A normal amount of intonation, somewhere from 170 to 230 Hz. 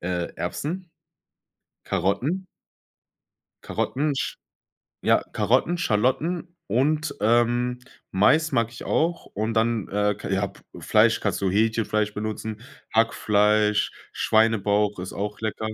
No: average, 3.8 semitones; low, 110 Hz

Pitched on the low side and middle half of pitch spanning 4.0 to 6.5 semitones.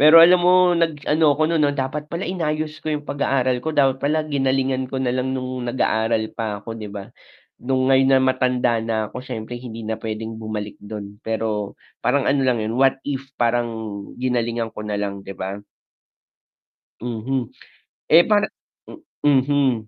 Yes: low, 130 Hz; average, 4.3 semitones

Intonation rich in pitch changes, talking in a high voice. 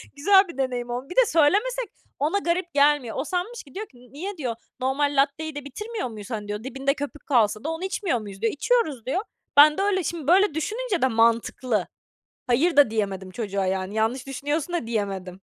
Yes: wide, 7.2 semitones; very high, 280 Hz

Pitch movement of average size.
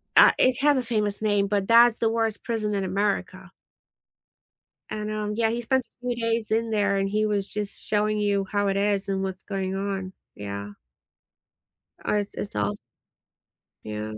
No: narrow, 2.3 semitones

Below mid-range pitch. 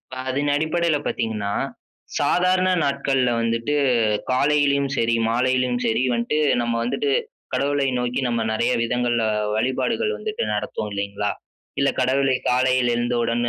Yes: low, 130 Hz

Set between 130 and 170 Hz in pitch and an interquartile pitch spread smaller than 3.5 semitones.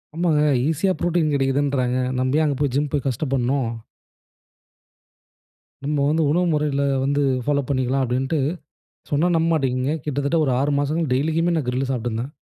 Yes: medium, 140 Hz; average, 2.8 semitones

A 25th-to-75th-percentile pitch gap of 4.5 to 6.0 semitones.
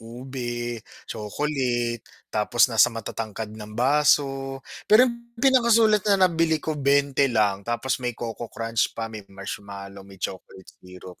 Yes: average, 5.3 semitones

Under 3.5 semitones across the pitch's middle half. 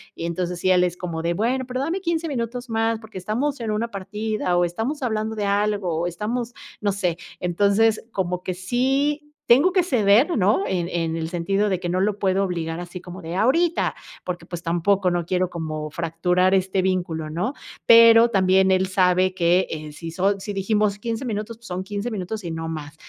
No: average, 4.1 semitones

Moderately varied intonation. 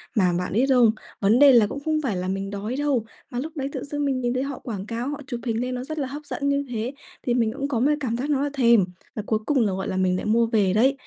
Yes: average, 4.4 semitones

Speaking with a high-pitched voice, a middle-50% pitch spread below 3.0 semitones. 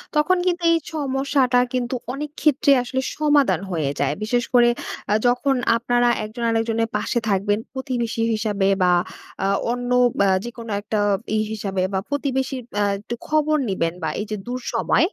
No: high, 240 Hz; average, 4.1 semitones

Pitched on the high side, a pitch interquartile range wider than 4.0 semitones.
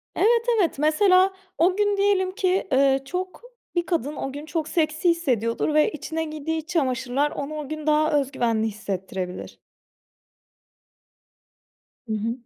Yes: very high, 310 Hz; average, 5.1 semitones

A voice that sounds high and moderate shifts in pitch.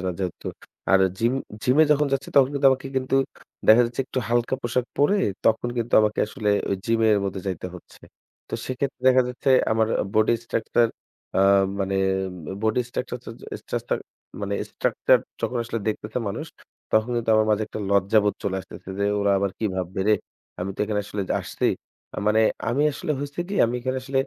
No: low, 115 Hz; average, 4.0 semitones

